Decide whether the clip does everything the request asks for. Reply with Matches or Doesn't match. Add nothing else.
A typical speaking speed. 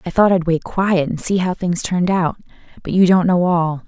Doesn't match